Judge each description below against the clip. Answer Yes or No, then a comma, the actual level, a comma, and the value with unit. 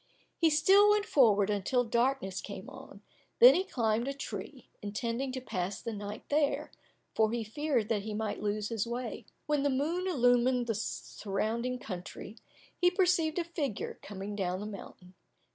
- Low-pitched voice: No, high, 235 Hz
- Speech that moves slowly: No, average, 165 wpm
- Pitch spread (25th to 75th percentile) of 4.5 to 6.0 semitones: Yes, wide, 5.6 semitones